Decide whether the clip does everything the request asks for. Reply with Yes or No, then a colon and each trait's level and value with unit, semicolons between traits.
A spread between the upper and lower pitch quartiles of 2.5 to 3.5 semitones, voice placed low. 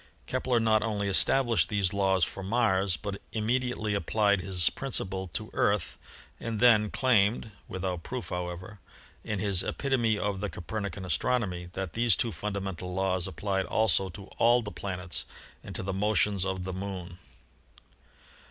Yes: average, 2.8 semitones; low, 100 Hz